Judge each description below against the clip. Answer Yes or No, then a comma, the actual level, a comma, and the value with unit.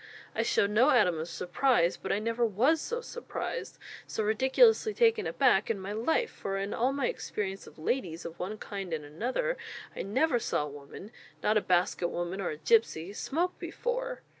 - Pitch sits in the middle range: No, high, 215 Hz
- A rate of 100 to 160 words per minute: No, average, 190 wpm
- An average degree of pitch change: No, wide, 7.3 semitones